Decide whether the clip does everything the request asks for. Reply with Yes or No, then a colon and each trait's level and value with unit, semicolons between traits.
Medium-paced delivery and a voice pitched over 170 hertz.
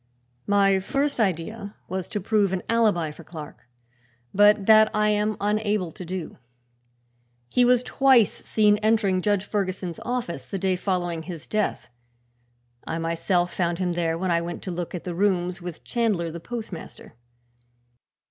Yes: average, 155 wpm; high, 190 Hz